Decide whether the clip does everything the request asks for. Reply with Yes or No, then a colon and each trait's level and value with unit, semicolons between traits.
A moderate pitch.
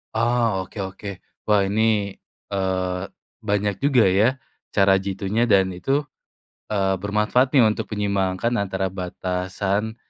No: low, 100 Hz